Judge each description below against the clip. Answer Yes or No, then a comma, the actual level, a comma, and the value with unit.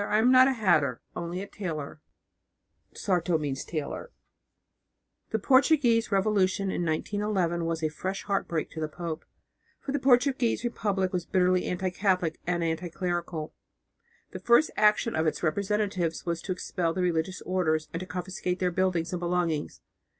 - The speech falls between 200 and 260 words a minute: No, average, 150 wpm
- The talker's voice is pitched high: No, medium, 180 Hz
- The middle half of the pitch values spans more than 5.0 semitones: No, average, 3.6 semitones